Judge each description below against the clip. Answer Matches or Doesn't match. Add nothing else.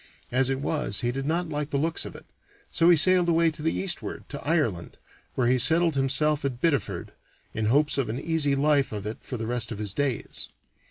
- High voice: Doesn't match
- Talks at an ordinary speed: Doesn't match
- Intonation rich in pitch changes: Doesn't match